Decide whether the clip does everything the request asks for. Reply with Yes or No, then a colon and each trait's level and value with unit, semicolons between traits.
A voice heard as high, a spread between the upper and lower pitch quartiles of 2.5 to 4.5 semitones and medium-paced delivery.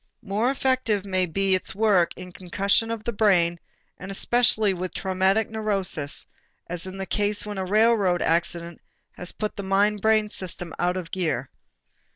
Yes: high, 195 Hz; average, 2.9 semitones; average, 165 wpm